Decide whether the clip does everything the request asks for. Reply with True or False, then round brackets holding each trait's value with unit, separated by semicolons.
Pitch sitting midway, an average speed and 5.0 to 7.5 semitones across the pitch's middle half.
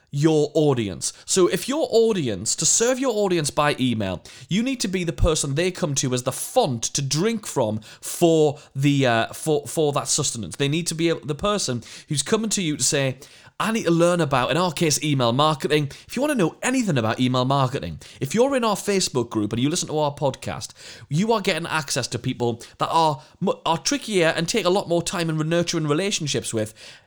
False (155 Hz; 215 wpm; 5.6 semitones)